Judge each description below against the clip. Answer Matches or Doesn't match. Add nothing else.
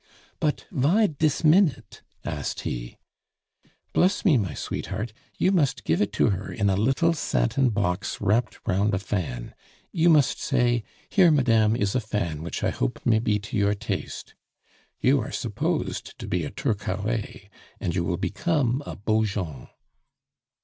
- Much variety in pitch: Matches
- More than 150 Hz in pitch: Doesn't match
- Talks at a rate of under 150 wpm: Doesn't match